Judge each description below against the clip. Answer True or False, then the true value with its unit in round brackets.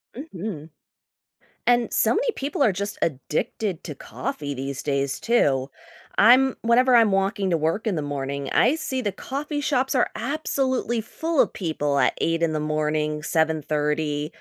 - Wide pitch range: True (8.4 semitones)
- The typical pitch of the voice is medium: True (180 Hz)